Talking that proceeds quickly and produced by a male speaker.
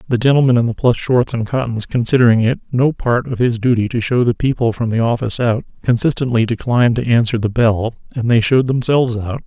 Yes: fast, 215 wpm; male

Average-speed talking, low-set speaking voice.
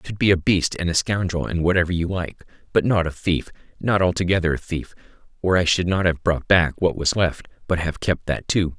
No: fast, 240 wpm; very low, 85 Hz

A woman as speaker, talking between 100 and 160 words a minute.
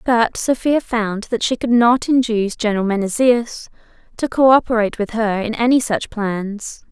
Yes: female; average, 155 wpm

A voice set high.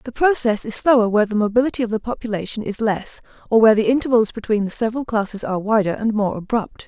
Yes: high, 220 Hz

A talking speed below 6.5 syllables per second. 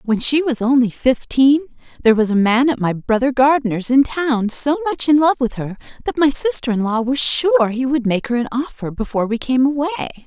Yes: 5.4 syllables/s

